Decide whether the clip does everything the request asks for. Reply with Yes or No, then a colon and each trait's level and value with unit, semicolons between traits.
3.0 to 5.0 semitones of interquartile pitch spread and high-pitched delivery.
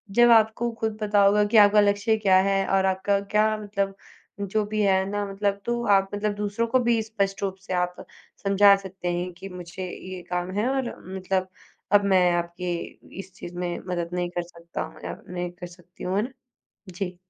No: narrow, 2.5 semitones; high, 195 Hz